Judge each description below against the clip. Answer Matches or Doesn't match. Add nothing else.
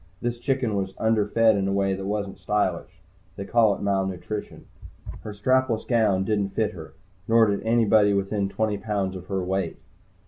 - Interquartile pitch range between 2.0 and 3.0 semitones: Matches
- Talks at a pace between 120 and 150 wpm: Doesn't match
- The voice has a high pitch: Doesn't match